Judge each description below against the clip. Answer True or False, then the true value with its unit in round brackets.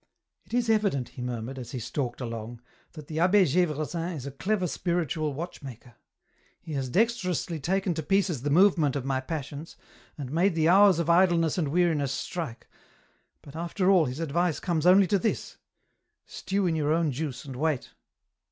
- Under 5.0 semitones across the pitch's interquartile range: True (4.5 semitones)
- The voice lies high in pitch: False (160 Hz)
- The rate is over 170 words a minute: True (185 wpm)